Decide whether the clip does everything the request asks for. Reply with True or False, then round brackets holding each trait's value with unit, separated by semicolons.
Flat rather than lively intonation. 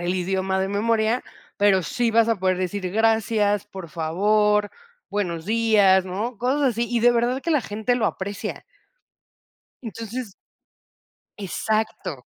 False (3.1 semitones)